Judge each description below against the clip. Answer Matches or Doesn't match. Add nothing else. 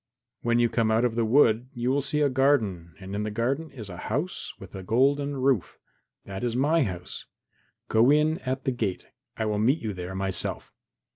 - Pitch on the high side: Doesn't match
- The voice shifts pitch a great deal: Doesn't match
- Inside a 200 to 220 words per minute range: Matches